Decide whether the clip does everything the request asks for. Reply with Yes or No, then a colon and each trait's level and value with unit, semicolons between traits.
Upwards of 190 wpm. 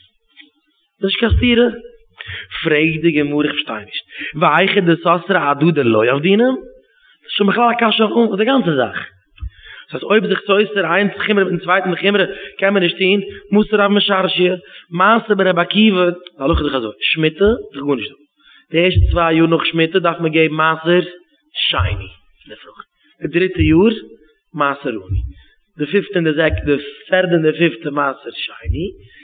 No: average, 160 wpm